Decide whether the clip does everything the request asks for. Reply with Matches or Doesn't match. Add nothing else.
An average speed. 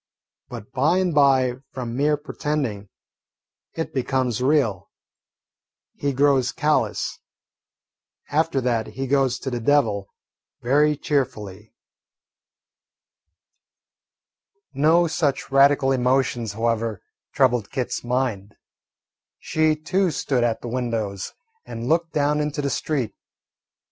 Doesn't match